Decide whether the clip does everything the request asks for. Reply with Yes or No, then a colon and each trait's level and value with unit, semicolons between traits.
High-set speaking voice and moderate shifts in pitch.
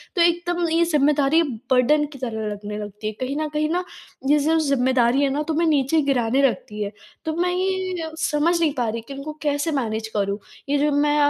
Yes: very high, 285 Hz; average, 4.6 semitones